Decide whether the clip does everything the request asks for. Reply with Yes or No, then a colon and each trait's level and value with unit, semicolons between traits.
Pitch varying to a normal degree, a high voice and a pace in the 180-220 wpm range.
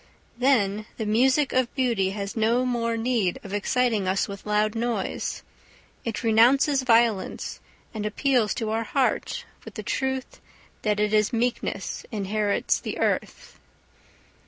No: average, 3.1 semitones; high, 225 Hz; slow, 135 wpm